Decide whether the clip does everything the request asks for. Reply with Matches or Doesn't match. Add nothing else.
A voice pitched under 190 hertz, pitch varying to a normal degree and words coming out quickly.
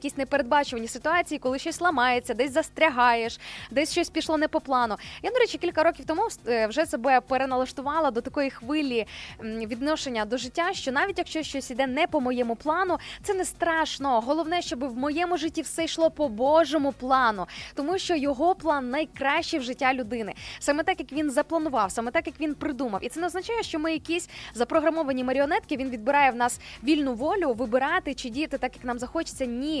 Doesn't match